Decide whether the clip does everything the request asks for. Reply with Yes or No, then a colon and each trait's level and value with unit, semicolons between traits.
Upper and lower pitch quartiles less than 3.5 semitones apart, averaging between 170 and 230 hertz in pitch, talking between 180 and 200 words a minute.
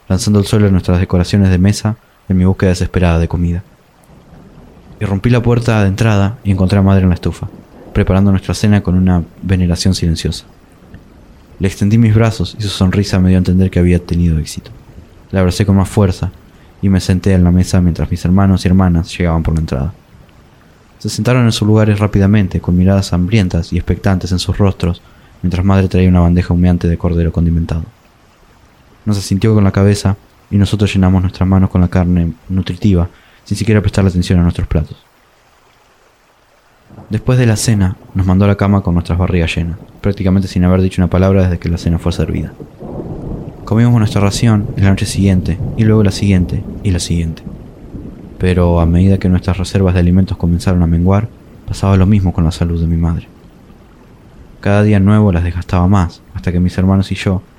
No: narrow, 2.4 semitones; very low, 95 Hz; fast, 190 wpm